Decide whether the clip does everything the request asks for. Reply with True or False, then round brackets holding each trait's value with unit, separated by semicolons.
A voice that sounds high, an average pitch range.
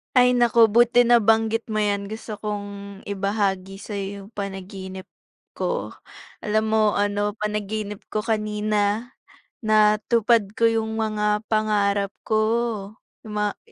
False (210 Hz; 1.6 semitones)